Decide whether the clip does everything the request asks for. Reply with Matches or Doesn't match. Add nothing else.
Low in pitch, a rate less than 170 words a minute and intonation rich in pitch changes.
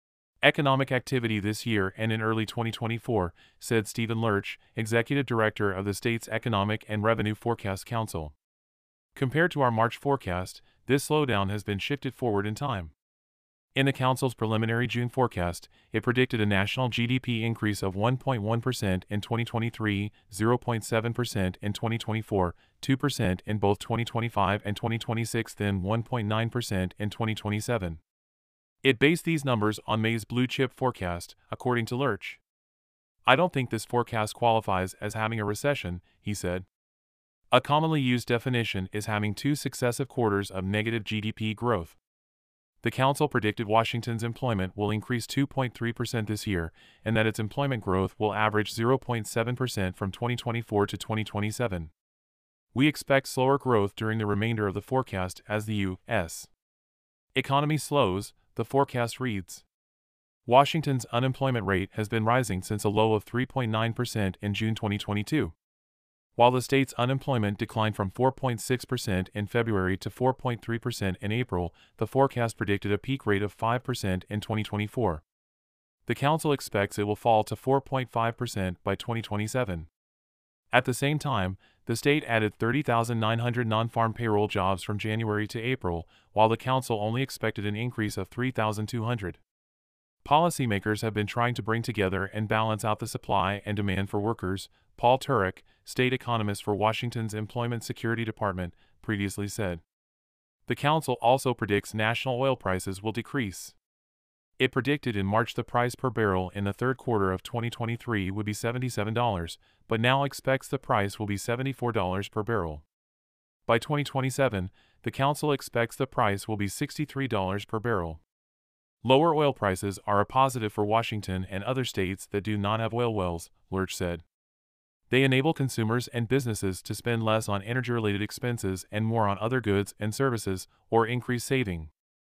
Doesn't match